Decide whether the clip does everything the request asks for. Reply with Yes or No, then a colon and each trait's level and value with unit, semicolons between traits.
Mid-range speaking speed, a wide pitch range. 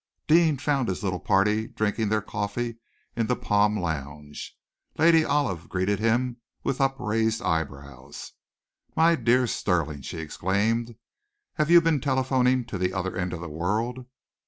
Yes: average, 145 wpm; wide, 5.9 semitones